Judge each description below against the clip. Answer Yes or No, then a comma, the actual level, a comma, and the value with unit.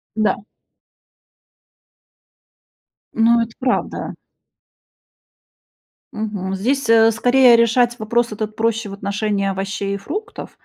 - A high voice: Yes, high, 225 Hz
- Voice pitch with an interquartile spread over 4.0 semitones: No, average, 2.8 semitones